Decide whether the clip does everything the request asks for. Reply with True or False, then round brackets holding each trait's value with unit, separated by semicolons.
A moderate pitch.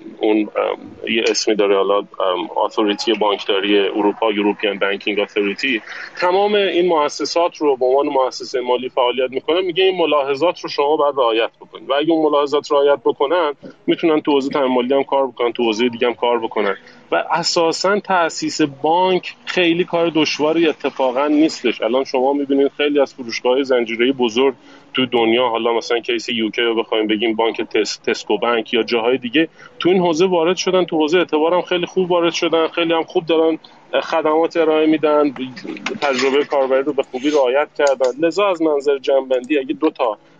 True (145 Hz)